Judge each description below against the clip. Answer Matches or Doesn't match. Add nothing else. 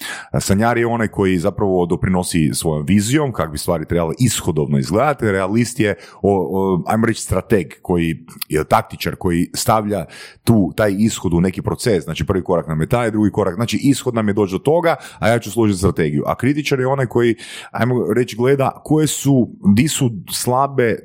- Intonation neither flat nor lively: Matches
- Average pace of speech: Doesn't match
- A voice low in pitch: Matches